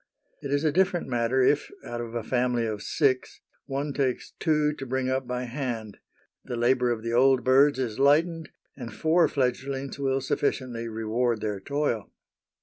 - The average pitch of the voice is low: Yes, low, 130 Hz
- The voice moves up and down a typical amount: Yes, average, 3.0 semitones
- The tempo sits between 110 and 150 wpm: No, average, 170 wpm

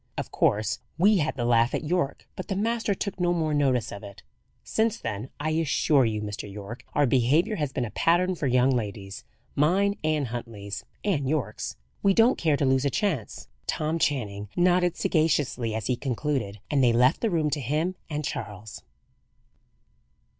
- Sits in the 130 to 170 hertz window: Yes, medium, 140 Hz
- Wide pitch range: Yes, wide, 6.4 semitones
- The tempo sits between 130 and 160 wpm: No, average, 180 wpm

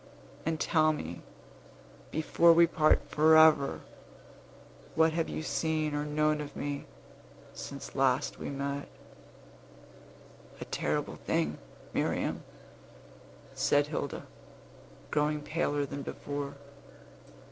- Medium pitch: Yes, medium, 150 Hz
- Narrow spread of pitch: Yes, narrow, 1.9 semitones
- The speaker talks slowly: Yes, slow, 100 wpm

